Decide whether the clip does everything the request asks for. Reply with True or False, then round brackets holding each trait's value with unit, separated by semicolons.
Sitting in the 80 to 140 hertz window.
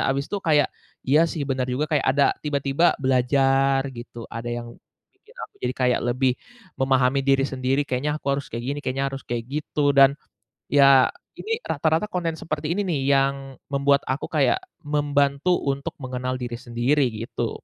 True (135 Hz)